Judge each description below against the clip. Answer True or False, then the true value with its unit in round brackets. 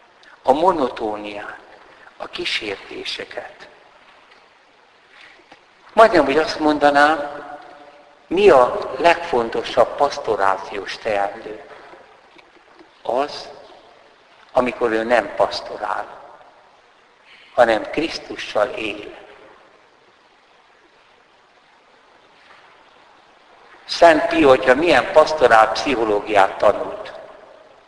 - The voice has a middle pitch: True (145 Hz)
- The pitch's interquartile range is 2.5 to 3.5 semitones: False (4.7 semitones)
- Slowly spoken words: True (60 wpm)